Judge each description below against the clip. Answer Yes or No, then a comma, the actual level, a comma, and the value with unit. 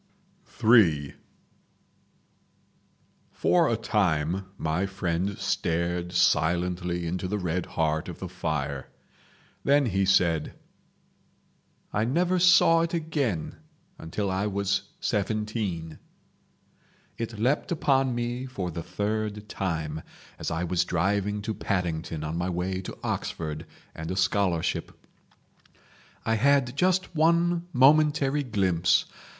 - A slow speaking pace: Yes, slow, 110 wpm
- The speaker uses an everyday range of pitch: No, wide, 6.0 semitones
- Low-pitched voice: Yes, very low, 95 Hz